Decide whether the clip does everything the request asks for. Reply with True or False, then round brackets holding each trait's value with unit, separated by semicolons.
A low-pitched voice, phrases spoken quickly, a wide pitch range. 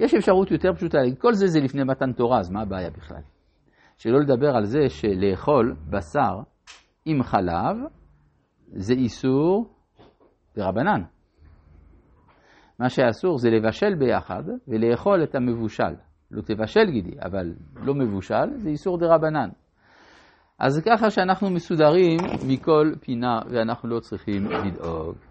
False (125 Hz; 125 wpm; 8.1 semitones)